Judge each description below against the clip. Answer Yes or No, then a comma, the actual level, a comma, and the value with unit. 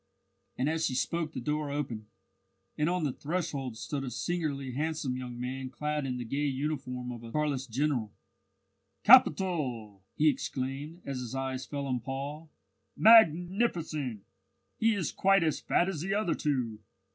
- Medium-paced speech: Yes, average, 160 wpm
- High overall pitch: No, medium, 140 Hz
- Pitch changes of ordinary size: Yes, average, 3.9 semitones